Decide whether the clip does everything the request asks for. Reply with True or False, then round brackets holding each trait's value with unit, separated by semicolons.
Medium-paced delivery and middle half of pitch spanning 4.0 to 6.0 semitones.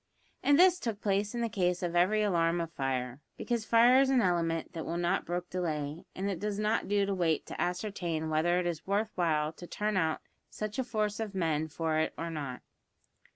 False (215 wpm; 4.5 semitones)